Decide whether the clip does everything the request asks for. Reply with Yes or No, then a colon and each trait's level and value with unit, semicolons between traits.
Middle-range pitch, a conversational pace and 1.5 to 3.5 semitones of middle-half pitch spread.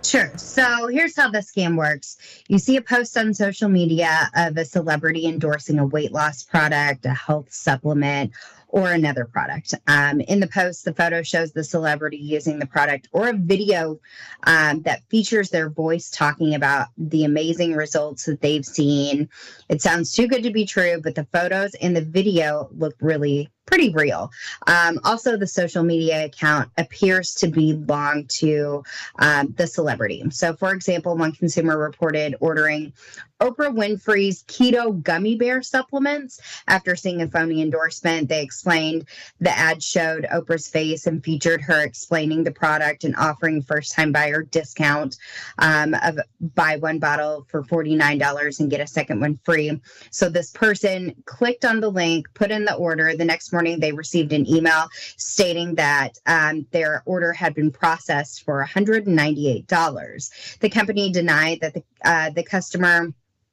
Yes: medium, 160 Hz; average, 160 wpm; average, 3.0 semitones